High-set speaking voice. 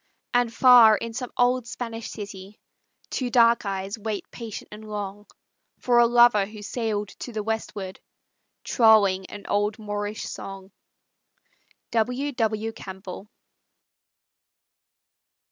Yes: high, 220 Hz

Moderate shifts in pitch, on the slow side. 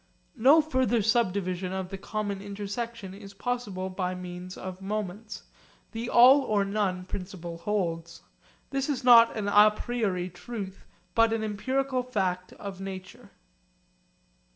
Yes: average, 3.9 semitones; slow, 130 wpm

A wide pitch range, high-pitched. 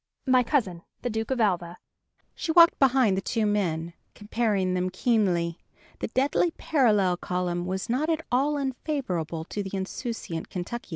Yes: wide, 6.1 semitones; high, 210 Hz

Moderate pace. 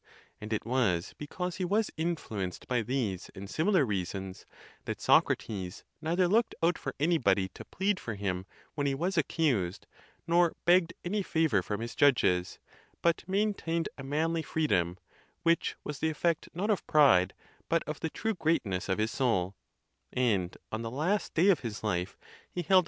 Yes: average, 170 wpm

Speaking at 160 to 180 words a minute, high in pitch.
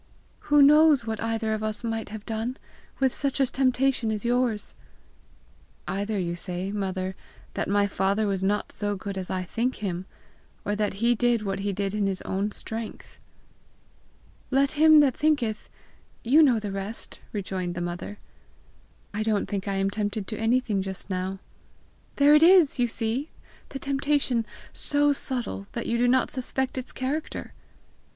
Yes: average, 170 wpm; high, 220 Hz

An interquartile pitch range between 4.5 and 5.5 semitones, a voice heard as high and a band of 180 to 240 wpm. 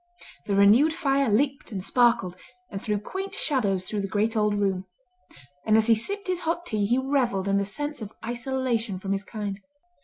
Yes: average, 5.2 semitones; high, 220 Hz; average, 190 wpm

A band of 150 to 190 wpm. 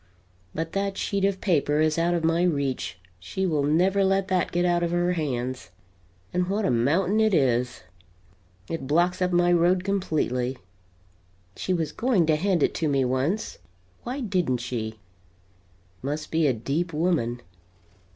Yes: average, 160 wpm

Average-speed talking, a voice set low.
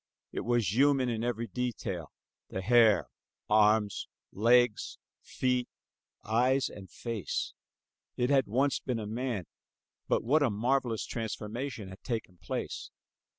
No: slow, 125 wpm; low, 115 Hz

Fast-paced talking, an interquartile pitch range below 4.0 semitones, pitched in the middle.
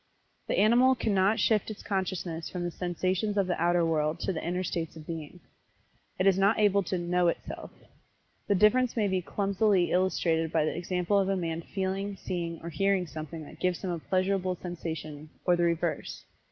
No: average, 190 wpm; average, 2.7 semitones; medium, 180 Hz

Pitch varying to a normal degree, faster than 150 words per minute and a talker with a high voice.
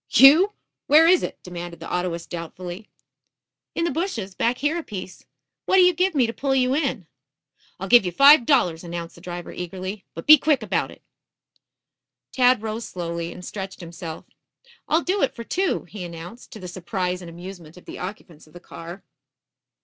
No: wide, 7.7 semitones; average, 185 wpm; high, 195 Hz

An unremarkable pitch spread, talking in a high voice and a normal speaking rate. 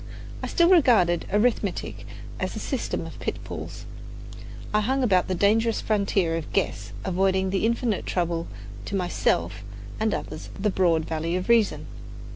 Yes: average, 4.1 semitones; high, 195 Hz; average, 145 wpm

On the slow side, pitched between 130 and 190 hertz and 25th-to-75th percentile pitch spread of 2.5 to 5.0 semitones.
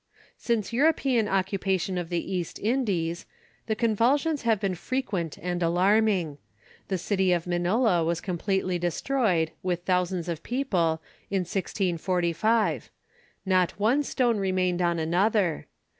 Yes: slow, 125 wpm; medium, 185 Hz; average, 4.0 semitones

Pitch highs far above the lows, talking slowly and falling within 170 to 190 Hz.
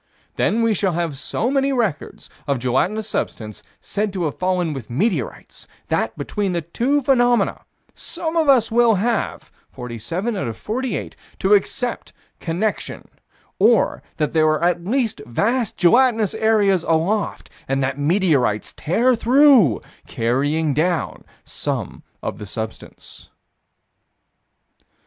Yes: wide, 7.8 semitones; slow, 120 wpm; medium, 185 Hz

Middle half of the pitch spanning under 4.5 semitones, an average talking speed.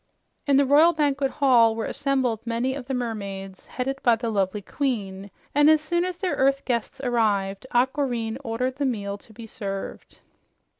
Yes: average, 4.1 semitones; average, 170 wpm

